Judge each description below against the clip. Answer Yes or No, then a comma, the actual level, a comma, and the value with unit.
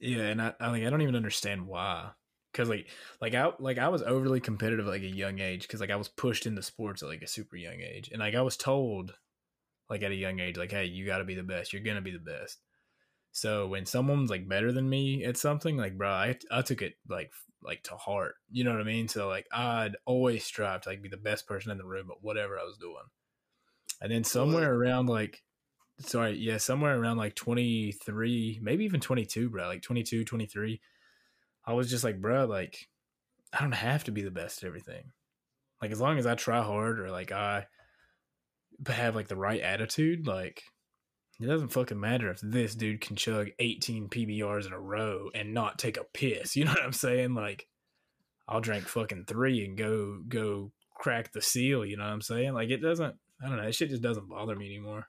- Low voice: Yes, low, 115 Hz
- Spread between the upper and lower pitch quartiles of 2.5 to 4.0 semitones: Yes, average, 3.5 semitones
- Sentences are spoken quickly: Yes, fast, 225 wpm